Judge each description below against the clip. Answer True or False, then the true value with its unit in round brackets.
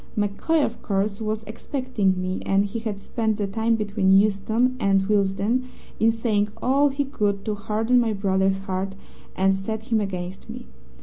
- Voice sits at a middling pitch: False (210 Hz)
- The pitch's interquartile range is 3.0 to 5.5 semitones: False (2.6 semitones)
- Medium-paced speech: True (170 wpm)